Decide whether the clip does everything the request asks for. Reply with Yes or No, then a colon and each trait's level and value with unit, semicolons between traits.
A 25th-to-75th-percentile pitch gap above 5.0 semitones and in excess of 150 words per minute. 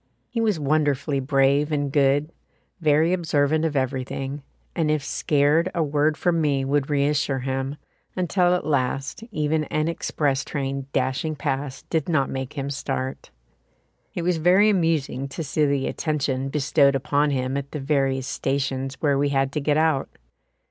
No: narrow, 2.4 semitones; average, 160 wpm